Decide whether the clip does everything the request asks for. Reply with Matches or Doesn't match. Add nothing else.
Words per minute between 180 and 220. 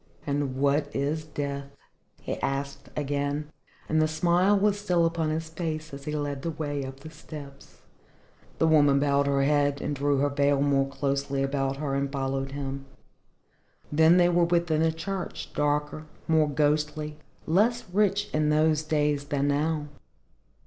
Doesn't match